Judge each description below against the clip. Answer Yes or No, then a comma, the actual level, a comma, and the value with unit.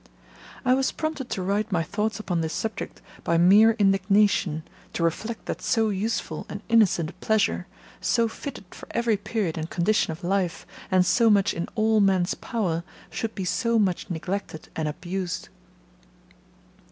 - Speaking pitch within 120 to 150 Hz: No, high, 200 Hz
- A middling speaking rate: Yes, average, 160 wpm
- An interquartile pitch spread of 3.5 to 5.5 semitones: Yes, average, 4.0 semitones